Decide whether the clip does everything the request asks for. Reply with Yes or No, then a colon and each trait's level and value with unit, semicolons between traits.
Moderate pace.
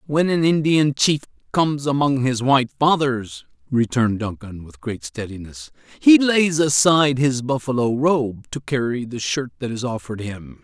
Yes: average, 160 wpm